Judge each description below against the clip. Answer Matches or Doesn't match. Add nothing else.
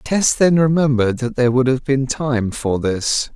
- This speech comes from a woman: Doesn't match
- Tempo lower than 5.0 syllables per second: Matches